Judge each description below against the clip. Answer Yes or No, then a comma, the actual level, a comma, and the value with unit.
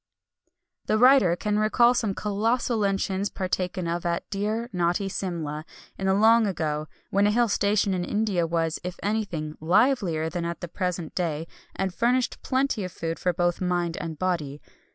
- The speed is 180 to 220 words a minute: No, average, 170 wpm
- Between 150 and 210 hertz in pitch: Yes, medium, 185 Hz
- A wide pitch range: No, average, 3.8 semitones